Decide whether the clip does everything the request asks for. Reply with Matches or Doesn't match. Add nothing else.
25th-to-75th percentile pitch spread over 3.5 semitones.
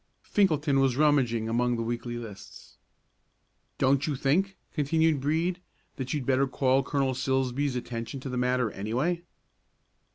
Doesn't match